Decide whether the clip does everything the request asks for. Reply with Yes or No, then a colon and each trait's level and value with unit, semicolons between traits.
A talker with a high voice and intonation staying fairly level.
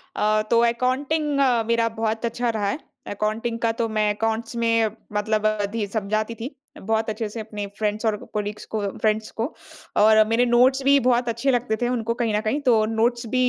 Yes: high, 225 Hz; narrow, 1.9 semitones